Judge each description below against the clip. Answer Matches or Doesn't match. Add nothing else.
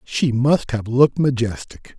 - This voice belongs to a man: Matches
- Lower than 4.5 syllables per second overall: Matches